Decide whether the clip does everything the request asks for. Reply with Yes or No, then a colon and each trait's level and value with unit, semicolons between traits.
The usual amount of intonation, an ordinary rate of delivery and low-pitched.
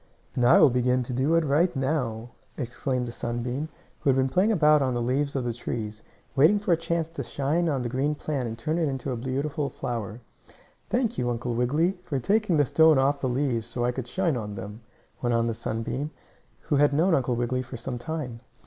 No: average, 4.1 semitones; fast, 220 wpm; low, 130 Hz